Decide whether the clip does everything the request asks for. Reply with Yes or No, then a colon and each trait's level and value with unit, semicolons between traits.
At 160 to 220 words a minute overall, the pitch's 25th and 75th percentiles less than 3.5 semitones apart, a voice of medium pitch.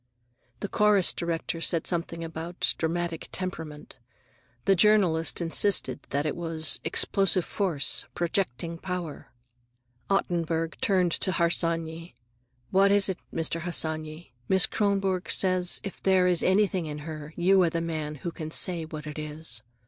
No: average, 140 wpm; narrow, 2.6 semitones; medium, 170 Hz